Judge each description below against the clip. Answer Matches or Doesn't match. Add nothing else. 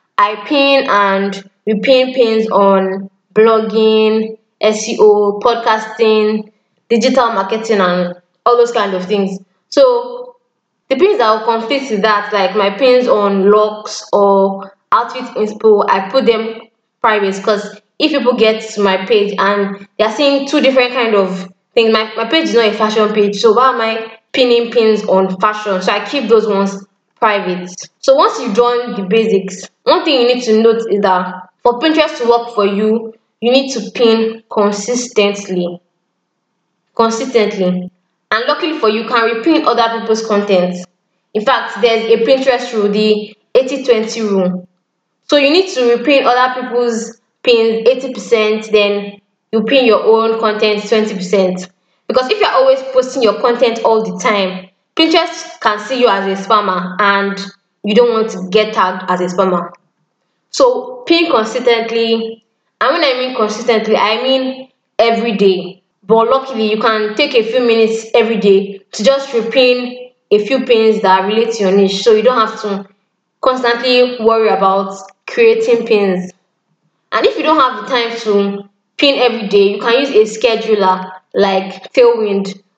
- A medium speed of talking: Matches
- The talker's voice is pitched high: Matches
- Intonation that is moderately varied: Matches